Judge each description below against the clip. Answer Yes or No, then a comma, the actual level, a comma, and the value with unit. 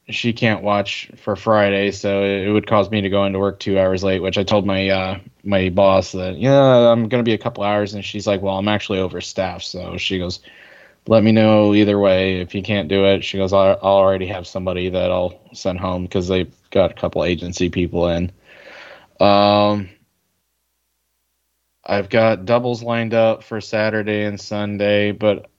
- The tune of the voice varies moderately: No, narrow, 2.2 semitones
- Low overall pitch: Yes, low, 100 Hz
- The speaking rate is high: No, average, 195 wpm